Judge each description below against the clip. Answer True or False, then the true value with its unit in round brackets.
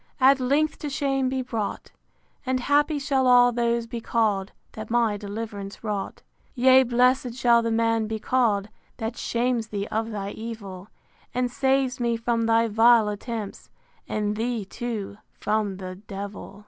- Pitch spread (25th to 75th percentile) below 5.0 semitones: True (3.0 semitones)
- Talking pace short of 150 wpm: False (160 wpm)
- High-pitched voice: True (230 Hz)